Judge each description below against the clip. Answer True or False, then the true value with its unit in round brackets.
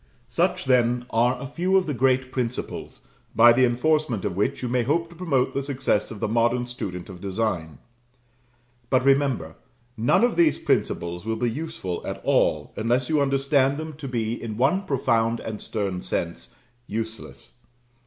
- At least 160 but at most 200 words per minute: True (170 wpm)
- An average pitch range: True (3.7 semitones)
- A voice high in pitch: False (125 Hz)